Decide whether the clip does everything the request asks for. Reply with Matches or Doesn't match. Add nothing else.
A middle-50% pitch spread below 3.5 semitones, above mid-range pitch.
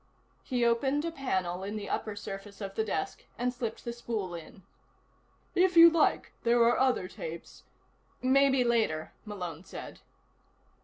Doesn't match